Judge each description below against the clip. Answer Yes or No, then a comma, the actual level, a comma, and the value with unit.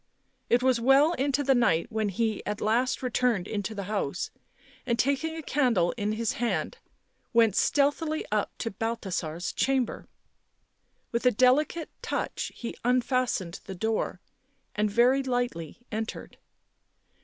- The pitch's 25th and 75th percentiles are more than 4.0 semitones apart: No, average, 3.7 semitones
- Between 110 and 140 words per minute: Yes, slow, 135 wpm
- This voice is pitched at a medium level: No, high, 235 Hz